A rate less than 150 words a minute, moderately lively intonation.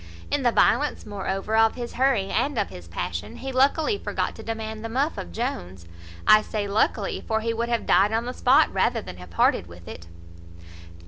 No: average, 200 wpm; average, 4.5 semitones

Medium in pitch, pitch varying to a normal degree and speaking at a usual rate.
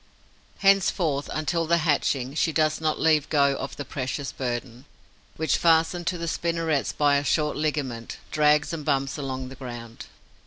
Yes: medium, 150 Hz; average, 3.0 semitones; average, 160 wpm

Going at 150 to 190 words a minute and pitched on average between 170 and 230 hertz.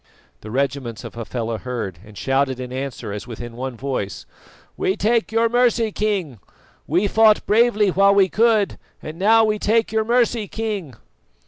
Yes: average, 160 wpm; high, 190 Hz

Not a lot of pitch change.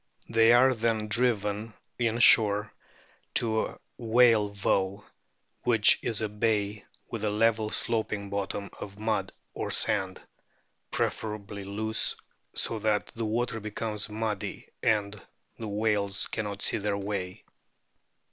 Yes: narrow, 1.8 semitones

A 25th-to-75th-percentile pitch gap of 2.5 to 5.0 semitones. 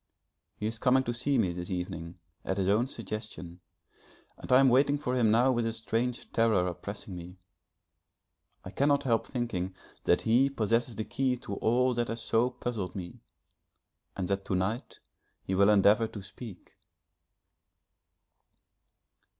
Yes: average, 4.4 semitones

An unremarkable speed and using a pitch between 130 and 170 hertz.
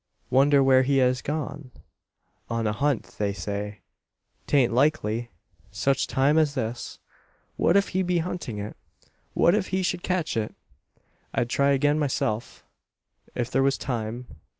Yes: average, 150 wpm; low, 135 Hz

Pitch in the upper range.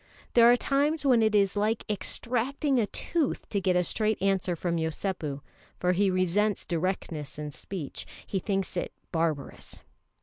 Yes: high, 195 Hz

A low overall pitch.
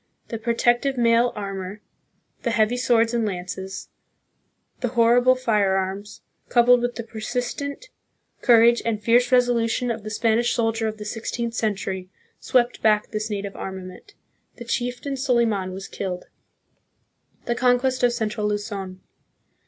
No: high, 230 Hz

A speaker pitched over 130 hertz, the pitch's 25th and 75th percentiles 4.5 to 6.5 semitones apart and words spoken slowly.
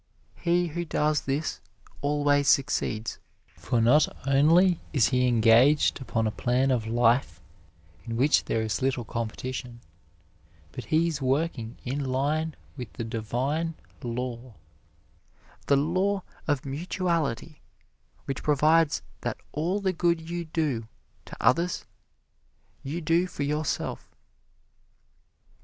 Yes: medium, 140 Hz; average, 4.8 semitones; slow, 120 wpm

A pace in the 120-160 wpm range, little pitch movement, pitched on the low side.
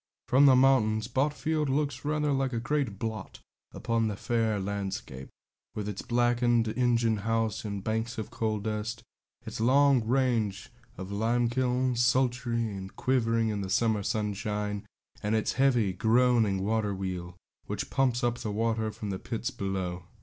No: average, 150 wpm; average, 3.1 semitones; low, 115 Hz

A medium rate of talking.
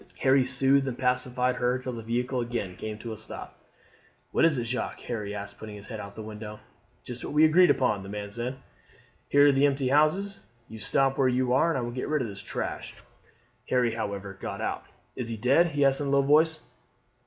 No: fast, 220 wpm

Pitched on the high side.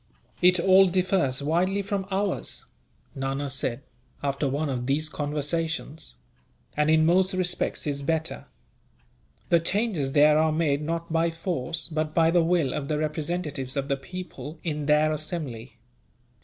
No: medium, 155 Hz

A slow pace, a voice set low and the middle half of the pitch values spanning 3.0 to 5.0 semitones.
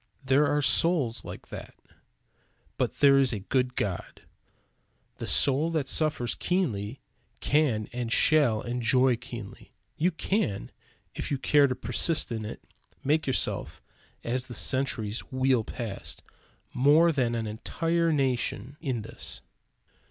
Yes: slow, 130 wpm; low, 130 Hz; average, 4.0 semitones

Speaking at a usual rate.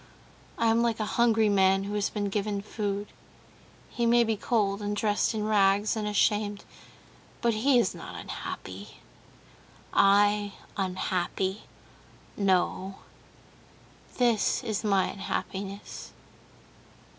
No: slow, 115 wpm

